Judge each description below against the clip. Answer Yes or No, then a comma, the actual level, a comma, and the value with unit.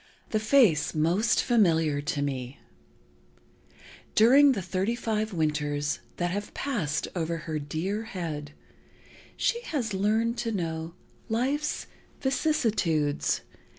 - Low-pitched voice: No, medium, 185 Hz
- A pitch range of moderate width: No, wide, 6.6 semitones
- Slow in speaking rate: Yes, slow, 110 wpm